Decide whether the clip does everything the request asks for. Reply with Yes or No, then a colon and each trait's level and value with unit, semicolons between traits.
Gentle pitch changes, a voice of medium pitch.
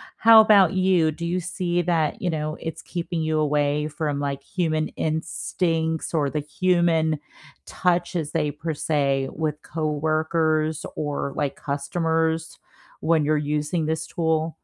Yes: narrow, 2.0 semitones; medium, 160 Hz